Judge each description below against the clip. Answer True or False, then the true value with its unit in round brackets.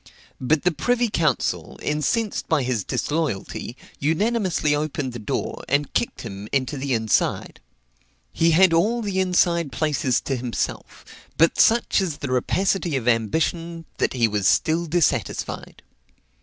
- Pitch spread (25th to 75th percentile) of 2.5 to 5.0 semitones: False (5.6 semitones)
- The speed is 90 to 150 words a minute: True (140 wpm)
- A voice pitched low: False (155 Hz)